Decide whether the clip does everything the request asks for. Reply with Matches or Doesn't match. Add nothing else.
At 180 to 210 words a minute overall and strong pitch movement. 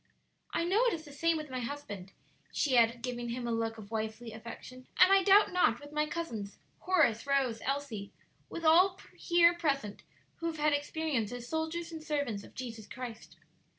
Matches